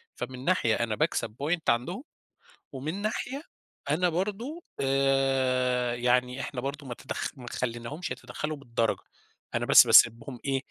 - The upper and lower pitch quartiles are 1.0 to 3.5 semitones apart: No, average, 4.2 semitones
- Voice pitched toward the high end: No, low, 135 Hz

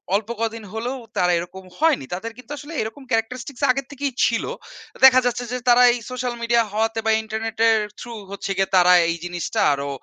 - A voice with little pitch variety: No, average, 3.3 semitones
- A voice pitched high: Yes, high, 225 Hz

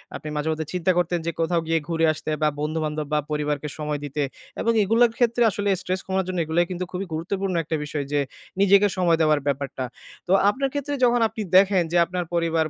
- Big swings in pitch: No, average, 4.1 semitones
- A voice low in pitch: No, medium, 170 Hz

